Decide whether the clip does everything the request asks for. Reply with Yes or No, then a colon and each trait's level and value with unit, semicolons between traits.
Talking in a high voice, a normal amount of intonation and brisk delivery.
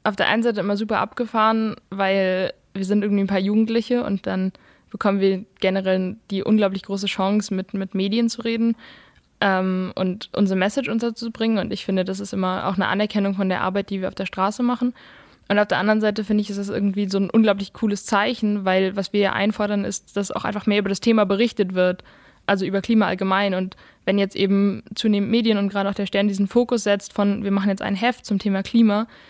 No: high, 200 Hz; narrow, 1.9 semitones; fast, 220 wpm